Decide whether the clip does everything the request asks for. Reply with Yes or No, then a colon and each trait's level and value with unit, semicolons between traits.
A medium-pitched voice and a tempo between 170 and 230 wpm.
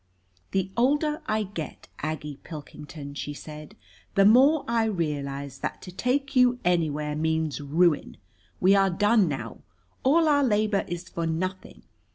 No: medium, 180 Hz; average, 150 wpm